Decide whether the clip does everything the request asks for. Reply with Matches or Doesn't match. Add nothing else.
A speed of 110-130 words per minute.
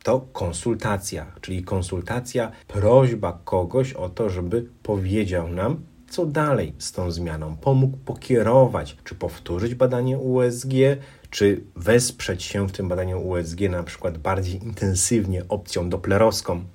Matches